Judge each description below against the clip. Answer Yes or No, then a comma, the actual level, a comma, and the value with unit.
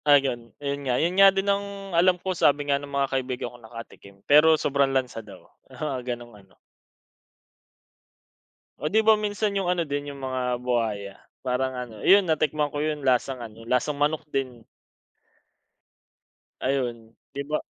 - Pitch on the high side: No, medium, 140 Hz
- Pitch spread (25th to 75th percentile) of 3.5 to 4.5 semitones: Yes, average, 4.2 semitones